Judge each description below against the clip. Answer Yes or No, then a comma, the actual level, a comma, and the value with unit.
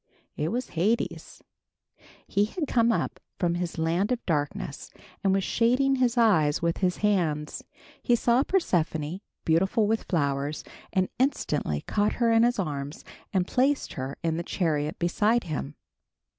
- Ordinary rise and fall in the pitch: No, wide, 6.6 semitones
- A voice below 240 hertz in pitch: Yes, medium, 185 Hz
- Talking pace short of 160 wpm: Yes, average, 150 wpm